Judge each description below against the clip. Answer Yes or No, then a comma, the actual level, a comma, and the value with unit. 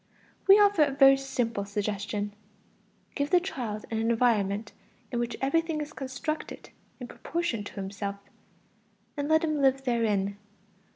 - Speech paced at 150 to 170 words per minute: No, slow, 135 wpm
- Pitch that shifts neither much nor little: No, wide, 6.1 semitones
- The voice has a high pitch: Yes, high, 245 Hz